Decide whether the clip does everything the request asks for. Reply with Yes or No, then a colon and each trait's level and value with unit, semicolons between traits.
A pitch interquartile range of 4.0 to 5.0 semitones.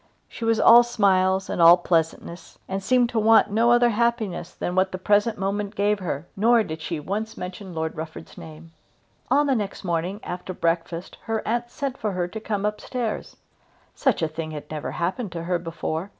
Yes: average, 4.7 semitones